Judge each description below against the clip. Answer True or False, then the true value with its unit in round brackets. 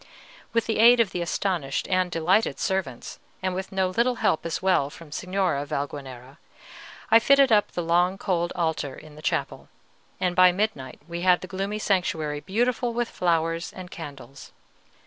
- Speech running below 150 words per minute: False (165 wpm)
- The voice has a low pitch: False (180 Hz)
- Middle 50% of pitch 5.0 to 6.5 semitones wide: False (3.9 semitones)